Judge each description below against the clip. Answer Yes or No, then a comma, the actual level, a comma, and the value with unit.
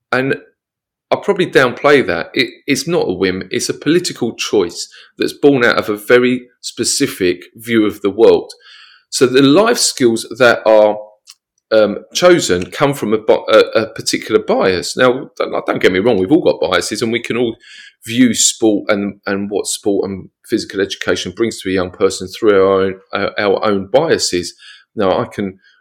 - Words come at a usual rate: Yes, average, 180 wpm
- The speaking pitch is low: Yes, low, 115 Hz